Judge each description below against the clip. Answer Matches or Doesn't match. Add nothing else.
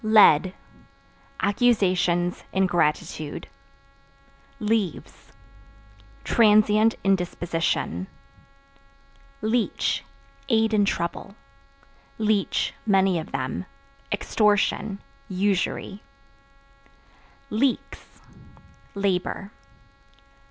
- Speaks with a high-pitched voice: Matches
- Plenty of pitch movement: Doesn't match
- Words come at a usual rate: Doesn't match